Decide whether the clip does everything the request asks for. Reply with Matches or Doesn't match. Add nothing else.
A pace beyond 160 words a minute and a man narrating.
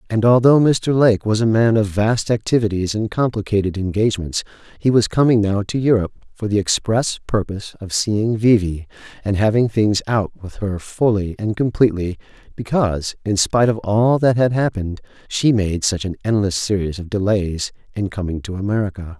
Matches